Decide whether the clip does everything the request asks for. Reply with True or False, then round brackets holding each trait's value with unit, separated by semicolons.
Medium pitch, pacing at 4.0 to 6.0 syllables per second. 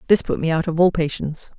False (165 Hz; 6.8 syllables/s)